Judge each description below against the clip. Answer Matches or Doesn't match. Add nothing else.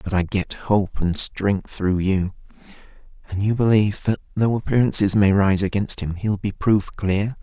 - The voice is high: Doesn't match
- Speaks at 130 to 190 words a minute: Matches